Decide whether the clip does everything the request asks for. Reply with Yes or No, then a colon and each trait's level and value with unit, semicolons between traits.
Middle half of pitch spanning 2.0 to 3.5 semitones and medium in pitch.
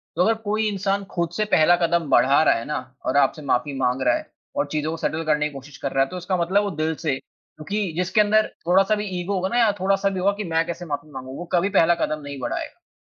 No: average, 4.8 semitones; medium, 170 Hz